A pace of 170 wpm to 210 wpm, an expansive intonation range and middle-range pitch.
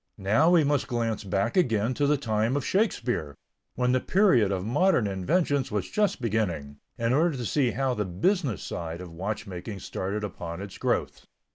No: average, 175 wpm; wide, 6.6 semitones; low, 115 Hz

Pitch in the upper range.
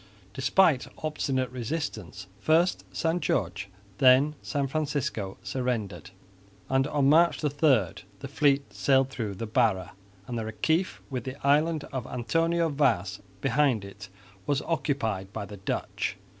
No: low, 130 Hz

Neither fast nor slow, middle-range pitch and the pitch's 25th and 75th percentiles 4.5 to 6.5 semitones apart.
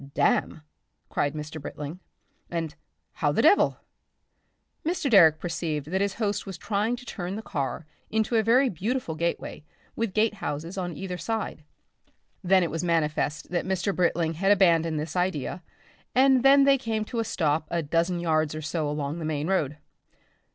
Yes: average, 170 wpm; medium, 175 Hz; average, 5.2 semitones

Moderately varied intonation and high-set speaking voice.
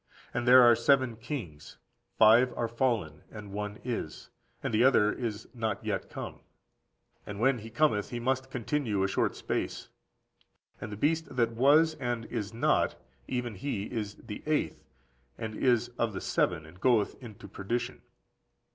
No: average, 3.5 semitones; low, 115 Hz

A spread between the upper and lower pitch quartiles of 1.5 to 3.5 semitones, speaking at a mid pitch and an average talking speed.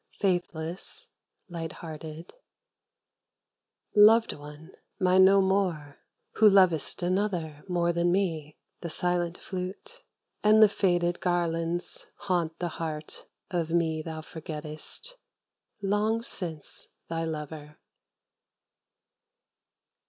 No: average, 3.0 semitones; medium, 175 Hz; slow, 95 wpm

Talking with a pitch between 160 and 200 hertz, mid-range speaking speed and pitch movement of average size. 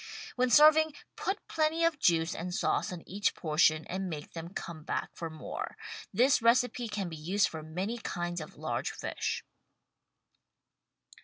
No: medium, 185 Hz; average, 155 wpm; wide, 7.1 semitones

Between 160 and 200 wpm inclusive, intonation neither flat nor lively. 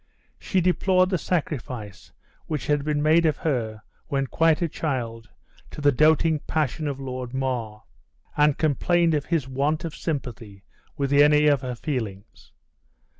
No: average, 150 wpm; average, 3.9 semitones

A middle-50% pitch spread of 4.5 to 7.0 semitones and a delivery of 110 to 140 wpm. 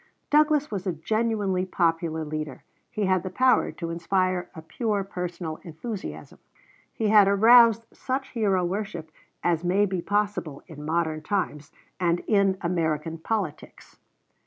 No: average, 4.1 semitones; slow, 135 wpm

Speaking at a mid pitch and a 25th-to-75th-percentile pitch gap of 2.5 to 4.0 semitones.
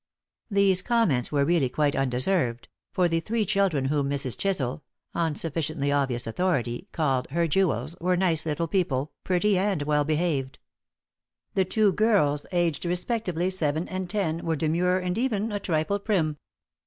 No: medium, 165 Hz; average, 4.6 semitones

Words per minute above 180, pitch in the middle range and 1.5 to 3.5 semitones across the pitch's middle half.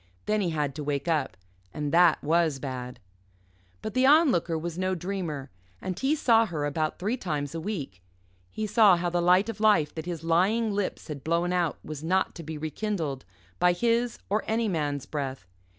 No: average, 190 wpm; medium, 170 Hz; wide, 5.4 semitones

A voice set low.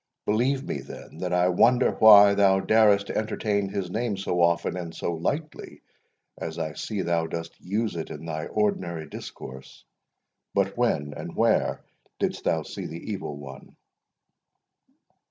Yes: very low, 90 Hz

